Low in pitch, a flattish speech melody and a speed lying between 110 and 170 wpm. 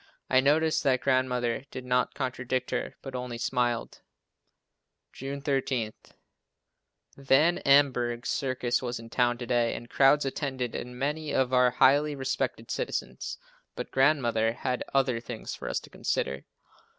Yes: low, 130 Hz; narrow, 2.2 semitones; average, 145 wpm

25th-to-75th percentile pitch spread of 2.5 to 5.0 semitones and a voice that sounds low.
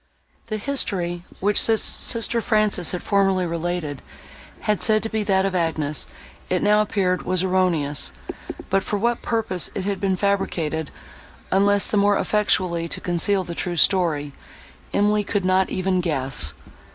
No: average, 3.0 semitones; high, 190 Hz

